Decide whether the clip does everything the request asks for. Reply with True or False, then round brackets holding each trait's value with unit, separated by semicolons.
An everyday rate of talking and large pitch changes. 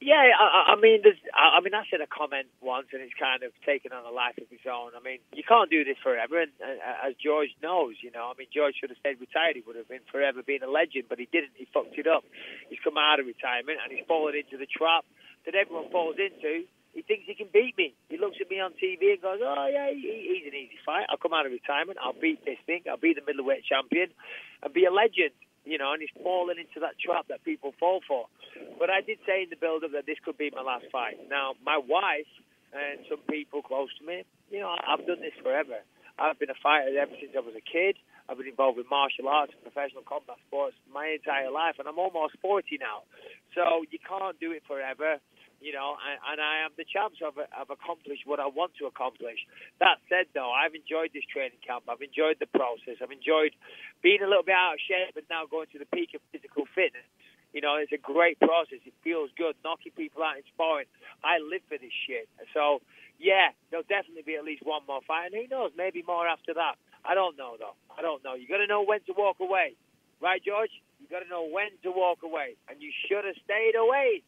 False (245 wpm; 6.8 semitones)